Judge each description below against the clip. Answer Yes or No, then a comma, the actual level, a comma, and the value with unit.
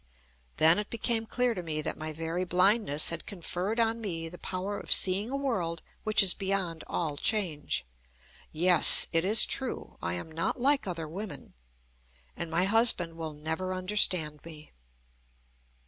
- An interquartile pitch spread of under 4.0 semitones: No, average, 4.4 semitones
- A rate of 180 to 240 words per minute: No, average, 160 wpm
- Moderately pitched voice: Yes, medium, 180 Hz